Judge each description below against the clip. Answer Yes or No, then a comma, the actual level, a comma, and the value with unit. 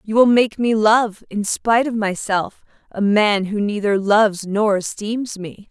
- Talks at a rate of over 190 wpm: No, average, 180 wpm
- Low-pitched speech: No, high, 210 Hz